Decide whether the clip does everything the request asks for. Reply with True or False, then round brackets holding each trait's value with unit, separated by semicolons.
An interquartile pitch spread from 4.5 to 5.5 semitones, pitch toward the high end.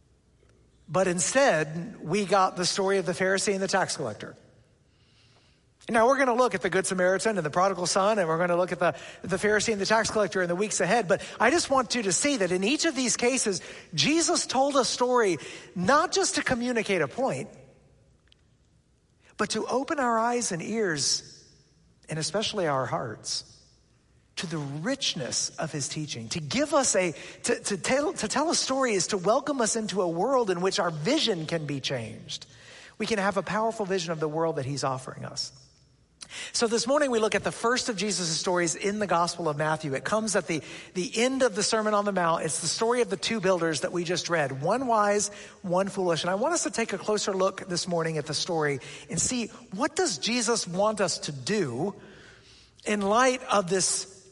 True (4.8 semitones; 195 Hz)